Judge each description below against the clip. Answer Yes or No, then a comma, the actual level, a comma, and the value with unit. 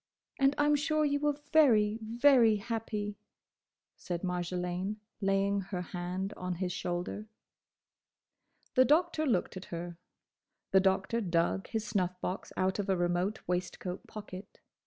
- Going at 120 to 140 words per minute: Yes, slow, 135 wpm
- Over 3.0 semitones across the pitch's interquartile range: Yes, average, 4.2 semitones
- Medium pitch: No, high, 195 Hz